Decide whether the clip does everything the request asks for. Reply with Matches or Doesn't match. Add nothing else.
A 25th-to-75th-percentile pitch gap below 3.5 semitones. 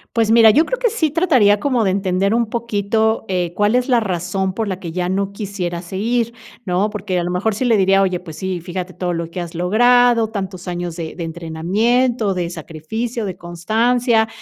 Doesn't match